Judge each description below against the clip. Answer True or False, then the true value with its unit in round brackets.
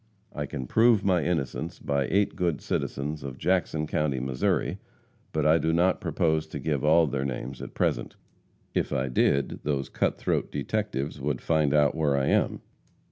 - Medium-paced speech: True (175 wpm)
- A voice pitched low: True (75 Hz)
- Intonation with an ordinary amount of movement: True (3.1 semitones)